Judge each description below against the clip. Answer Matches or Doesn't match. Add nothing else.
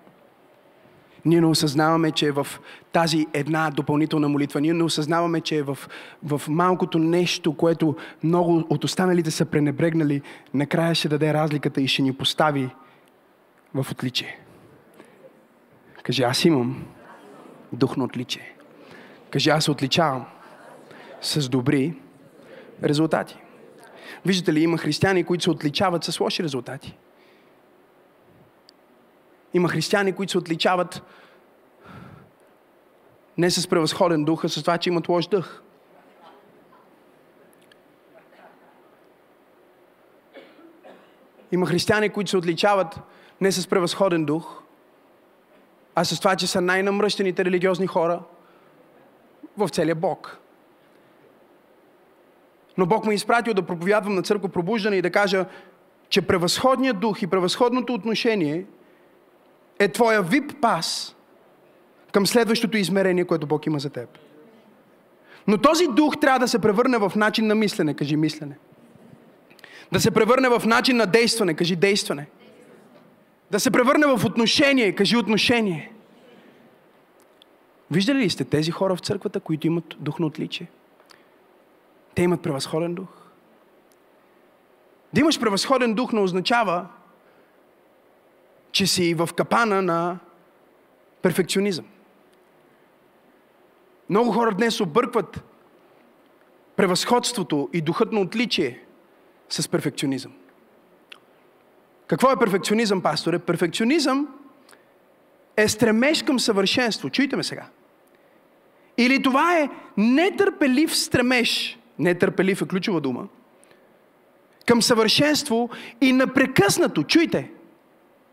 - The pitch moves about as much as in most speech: Doesn't match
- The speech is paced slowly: Matches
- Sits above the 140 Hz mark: Matches